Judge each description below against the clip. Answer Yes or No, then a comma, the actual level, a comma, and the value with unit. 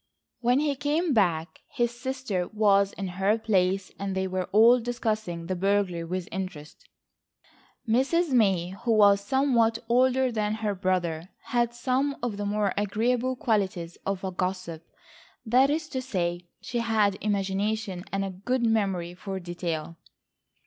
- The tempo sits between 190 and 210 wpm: No, average, 150 wpm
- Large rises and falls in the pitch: No, average, 4.4 semitones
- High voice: Yes, high, 205 Hz